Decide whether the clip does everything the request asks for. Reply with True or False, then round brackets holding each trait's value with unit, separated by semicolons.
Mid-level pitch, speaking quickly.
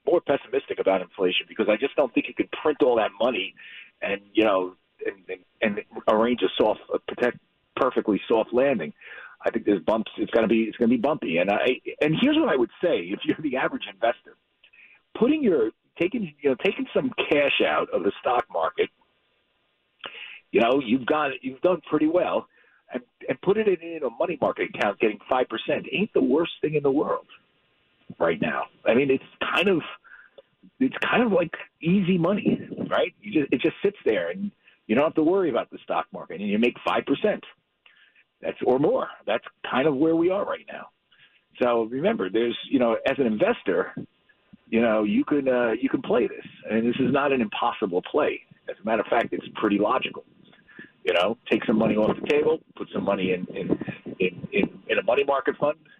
True (175 Hz; 210 wpm)